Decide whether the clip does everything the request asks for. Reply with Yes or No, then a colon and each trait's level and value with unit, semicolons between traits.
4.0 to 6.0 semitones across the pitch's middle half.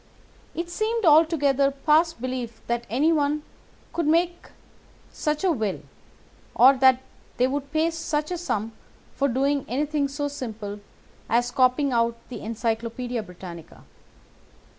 Yes: average, 4.3 semitones